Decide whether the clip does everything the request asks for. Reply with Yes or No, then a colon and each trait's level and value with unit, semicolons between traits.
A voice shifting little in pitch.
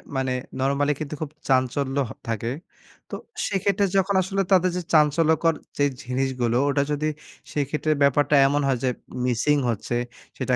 No: average, 3.0 semitones